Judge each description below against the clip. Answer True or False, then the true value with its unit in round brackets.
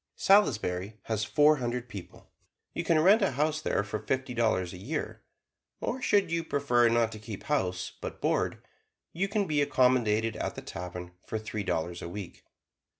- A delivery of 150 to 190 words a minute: True (175 wpm)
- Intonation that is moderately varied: False (6.8 semitones)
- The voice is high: False (120 Hz)